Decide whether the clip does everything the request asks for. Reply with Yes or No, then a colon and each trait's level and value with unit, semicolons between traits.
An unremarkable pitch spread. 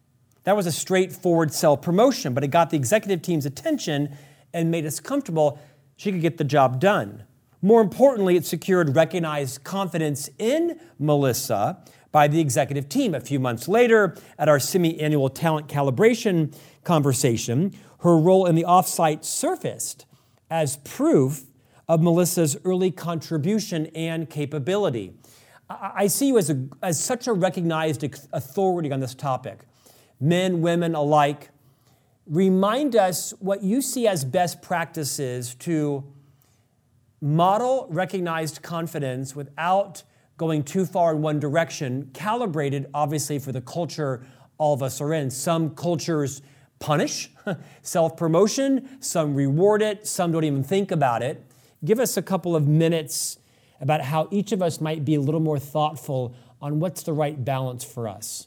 Yes: average, 4.6 semitones